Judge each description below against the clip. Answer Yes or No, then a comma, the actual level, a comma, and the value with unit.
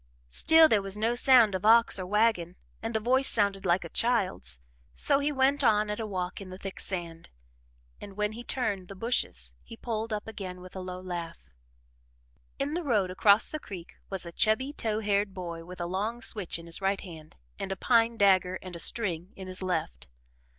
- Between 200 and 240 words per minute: Yes, fast, 205 wpm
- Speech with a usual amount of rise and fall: Yes, average, 3.8 semitones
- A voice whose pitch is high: Yes, high, 200 Hz